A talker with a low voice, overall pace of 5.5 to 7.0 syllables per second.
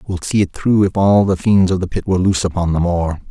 Yes: very low, 95 Hz; 6.2 syllables/s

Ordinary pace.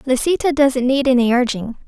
Yes: average, 160 wpm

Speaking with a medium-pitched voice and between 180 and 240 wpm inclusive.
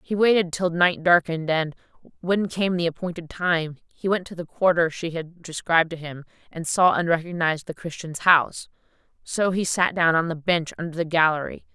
Yes: medium, 170 Hz; average, 195 wpm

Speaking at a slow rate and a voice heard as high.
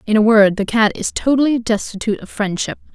No: fast, 205 wpm; high, 220 Hz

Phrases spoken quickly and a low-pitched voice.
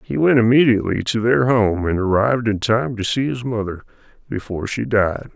No: average, 190 wpm; low, 115 Hz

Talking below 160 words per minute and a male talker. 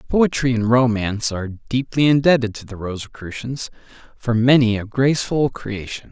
Yes: slow, 135 wpm; male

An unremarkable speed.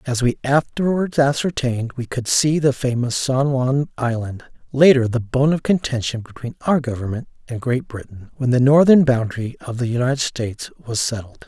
Yes: average, 175 wpm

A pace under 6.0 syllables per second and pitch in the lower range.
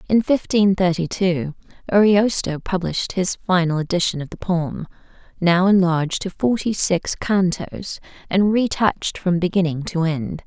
No: 4.5 syllables/s; medium, 180 Hz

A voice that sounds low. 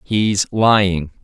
Yes: low, 100 Hz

